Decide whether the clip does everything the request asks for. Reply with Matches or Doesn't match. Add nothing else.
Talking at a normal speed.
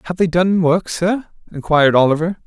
Matches